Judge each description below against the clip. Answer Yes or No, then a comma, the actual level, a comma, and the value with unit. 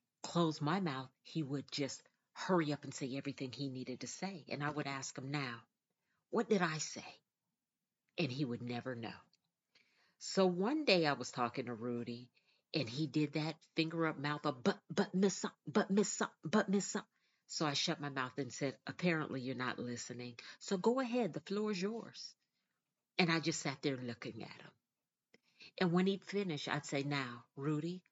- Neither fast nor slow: Yes, average, 190 wpm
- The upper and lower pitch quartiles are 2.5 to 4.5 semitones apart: No, wide, 5.5 semitones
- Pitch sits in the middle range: Yes, medium, 150 Hz